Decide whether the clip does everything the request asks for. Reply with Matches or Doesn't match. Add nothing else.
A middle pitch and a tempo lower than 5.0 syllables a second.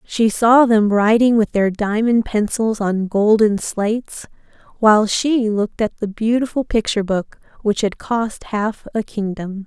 Doesn't match